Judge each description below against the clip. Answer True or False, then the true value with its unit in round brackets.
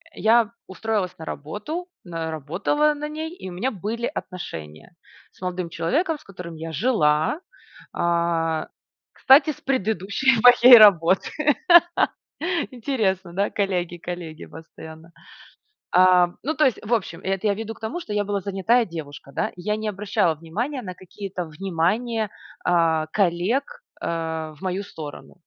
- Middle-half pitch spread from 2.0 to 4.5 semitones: False (5.2 semitones)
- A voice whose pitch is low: False (190 Hz)